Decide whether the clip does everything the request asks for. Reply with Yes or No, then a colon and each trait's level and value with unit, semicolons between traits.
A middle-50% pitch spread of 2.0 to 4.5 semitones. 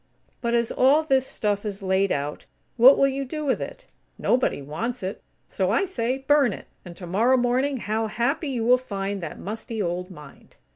No: average, 5.2 semitones